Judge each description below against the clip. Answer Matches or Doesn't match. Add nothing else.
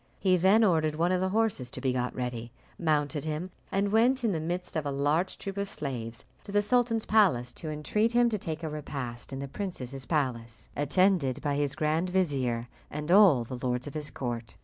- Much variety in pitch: Matches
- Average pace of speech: Doesn't match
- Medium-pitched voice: Matches